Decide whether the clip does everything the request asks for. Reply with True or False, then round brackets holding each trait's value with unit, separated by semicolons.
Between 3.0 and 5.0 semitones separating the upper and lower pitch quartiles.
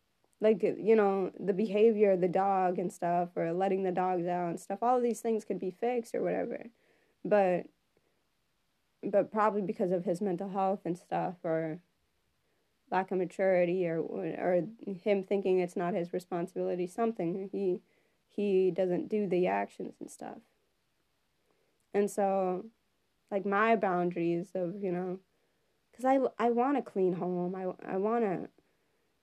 False (2.6 semitones)